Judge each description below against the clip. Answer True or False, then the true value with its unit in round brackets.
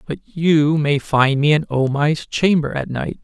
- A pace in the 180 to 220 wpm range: True (205 wpm)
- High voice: False (150 Hz)